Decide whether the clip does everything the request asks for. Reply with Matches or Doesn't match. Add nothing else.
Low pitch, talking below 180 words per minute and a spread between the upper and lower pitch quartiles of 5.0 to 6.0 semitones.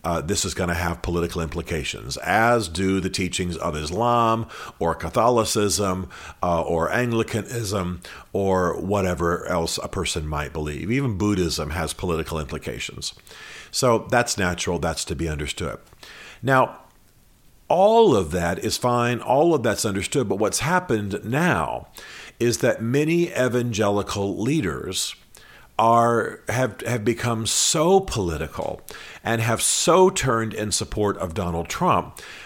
Matches